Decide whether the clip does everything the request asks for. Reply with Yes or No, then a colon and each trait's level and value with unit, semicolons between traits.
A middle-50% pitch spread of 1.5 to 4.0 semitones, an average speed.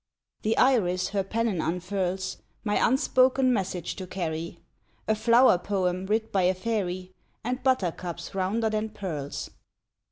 No: average, 3.7 semitones; slow, 130 wpm